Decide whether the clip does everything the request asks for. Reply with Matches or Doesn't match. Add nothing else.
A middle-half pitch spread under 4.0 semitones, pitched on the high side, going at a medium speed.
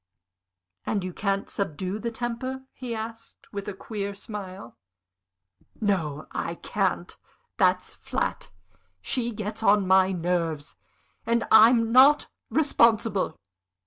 Doesn't match